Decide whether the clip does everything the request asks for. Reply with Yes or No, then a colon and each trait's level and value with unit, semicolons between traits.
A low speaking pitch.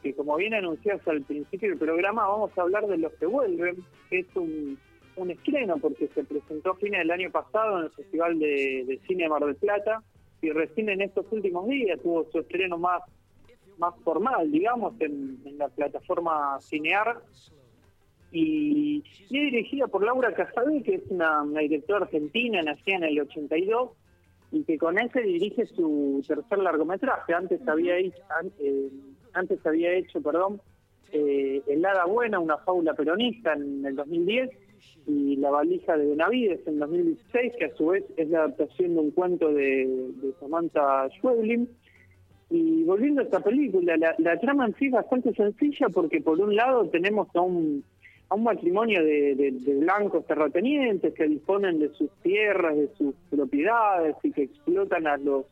No: medium, 170 Hz